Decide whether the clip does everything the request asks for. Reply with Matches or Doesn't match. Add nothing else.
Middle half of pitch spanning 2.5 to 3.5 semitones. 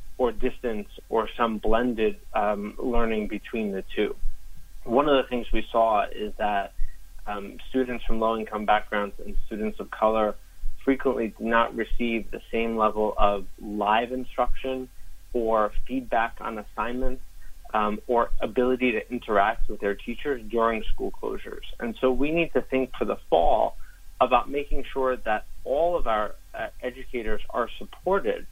Matches